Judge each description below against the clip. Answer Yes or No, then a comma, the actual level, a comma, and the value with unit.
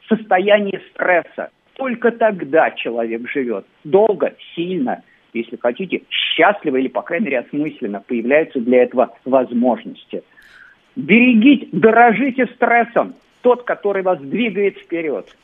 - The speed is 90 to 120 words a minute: Yes, slow, 110 wpm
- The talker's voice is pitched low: No, high, 195 Hz